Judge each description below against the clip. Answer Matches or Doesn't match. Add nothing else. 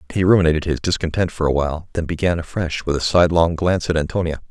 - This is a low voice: Matches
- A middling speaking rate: Doesn't match